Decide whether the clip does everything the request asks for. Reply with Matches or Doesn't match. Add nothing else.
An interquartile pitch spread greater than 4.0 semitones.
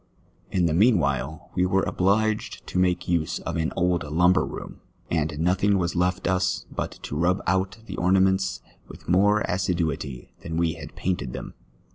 Doesn't match